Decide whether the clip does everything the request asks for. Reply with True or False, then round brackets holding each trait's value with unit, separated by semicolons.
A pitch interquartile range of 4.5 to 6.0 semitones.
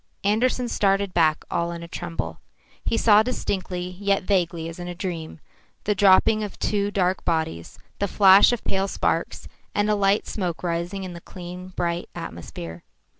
False (2.8 semitones)